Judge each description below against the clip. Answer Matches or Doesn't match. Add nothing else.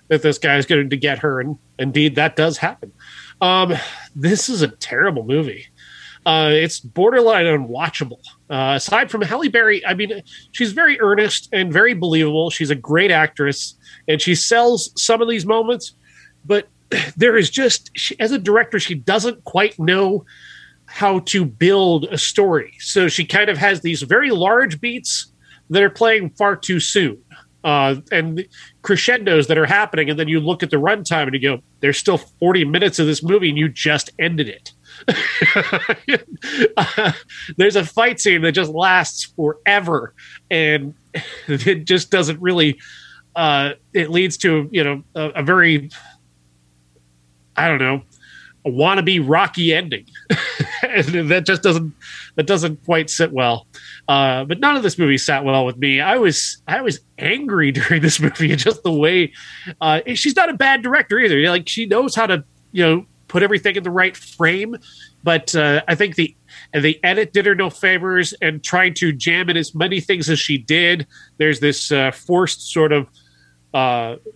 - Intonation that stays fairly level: Doesn't match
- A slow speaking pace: Doesn't match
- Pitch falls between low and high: Matches